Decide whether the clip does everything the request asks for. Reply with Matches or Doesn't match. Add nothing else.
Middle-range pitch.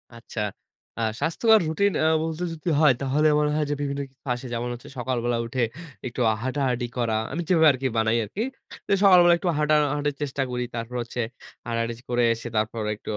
Doesn't match